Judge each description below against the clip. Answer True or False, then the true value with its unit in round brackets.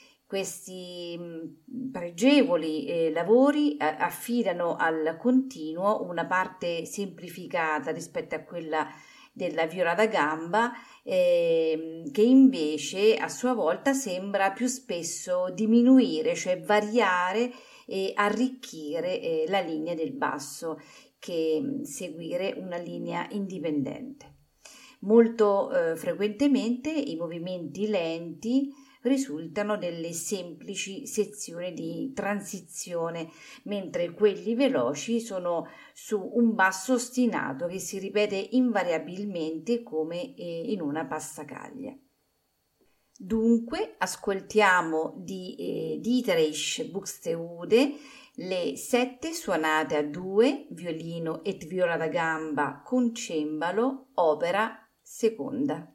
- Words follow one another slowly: True (95 wpm)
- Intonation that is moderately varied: False (6.8 semitones)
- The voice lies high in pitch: True (195 Hz)